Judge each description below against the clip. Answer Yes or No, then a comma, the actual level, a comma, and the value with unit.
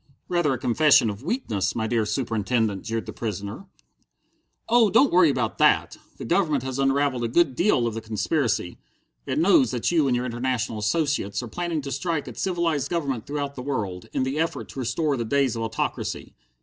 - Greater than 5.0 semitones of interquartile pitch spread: Yes, wide, 5.4 semitones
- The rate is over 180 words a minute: Yes, average, 190 wpm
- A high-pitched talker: No, low, 130 Hz